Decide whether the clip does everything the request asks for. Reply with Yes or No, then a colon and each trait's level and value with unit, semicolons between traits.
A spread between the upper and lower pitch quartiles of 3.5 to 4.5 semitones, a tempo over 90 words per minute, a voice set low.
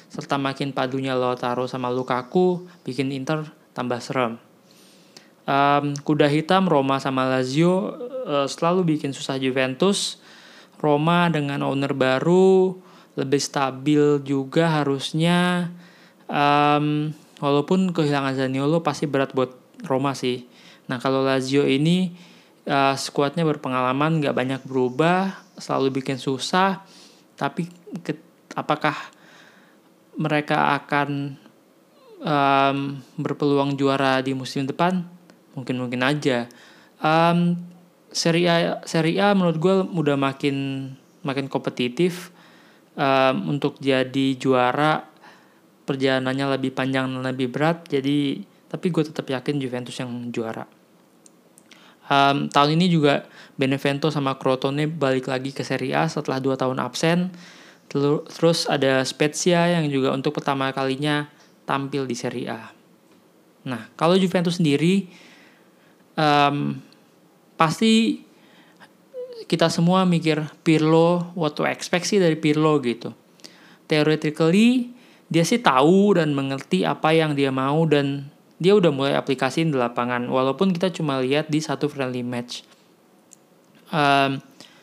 No: average, 3.8 semitones; average, 120 wpm; medium, 145 Hz